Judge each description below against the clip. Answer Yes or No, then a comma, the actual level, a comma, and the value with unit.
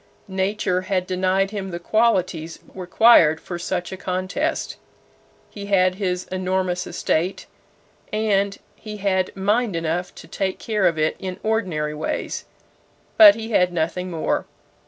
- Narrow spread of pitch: Yes, narrow, 2.2 semitones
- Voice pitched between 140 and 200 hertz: Yes, medium, 185 Hz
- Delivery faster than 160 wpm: No, slow, 135 wpm